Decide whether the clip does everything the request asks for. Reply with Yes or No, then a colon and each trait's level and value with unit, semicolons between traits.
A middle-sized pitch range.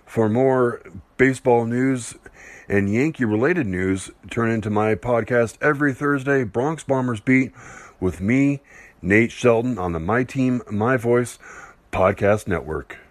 Yes: average, 3.8 semitones